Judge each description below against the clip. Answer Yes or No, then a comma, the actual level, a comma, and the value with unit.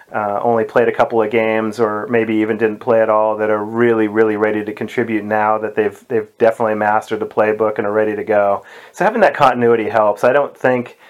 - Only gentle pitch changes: Yes, narrow, 1.0 semitones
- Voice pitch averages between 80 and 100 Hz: No, low, 110 Hz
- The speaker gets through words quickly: Yes, fast, 225 wpm